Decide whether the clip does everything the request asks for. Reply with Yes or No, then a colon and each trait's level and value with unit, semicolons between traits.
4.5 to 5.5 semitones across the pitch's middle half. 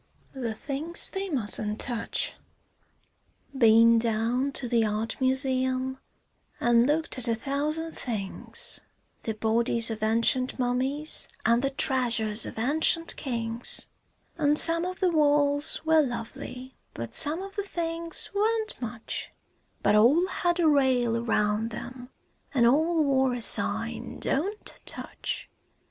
Yes: average, 4.9 semitones